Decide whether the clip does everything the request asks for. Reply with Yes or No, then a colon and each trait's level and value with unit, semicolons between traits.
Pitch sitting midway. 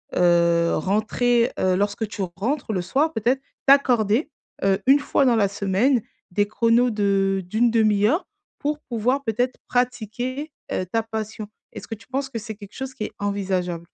No: high, 220 Hz